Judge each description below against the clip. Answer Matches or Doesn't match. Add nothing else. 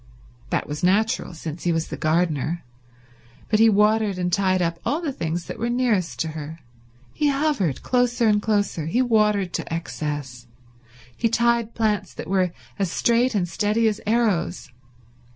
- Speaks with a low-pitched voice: Doesn't match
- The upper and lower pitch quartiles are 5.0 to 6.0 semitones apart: Matches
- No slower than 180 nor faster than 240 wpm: Doesn't match